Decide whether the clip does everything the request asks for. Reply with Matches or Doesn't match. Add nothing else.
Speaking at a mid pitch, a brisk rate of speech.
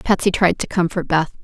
Matches